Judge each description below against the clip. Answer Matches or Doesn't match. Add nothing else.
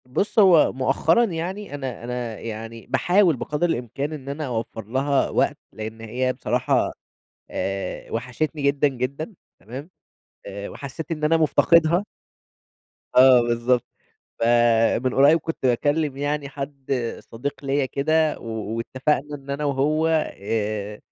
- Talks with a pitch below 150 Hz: Matches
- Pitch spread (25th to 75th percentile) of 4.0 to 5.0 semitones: Matches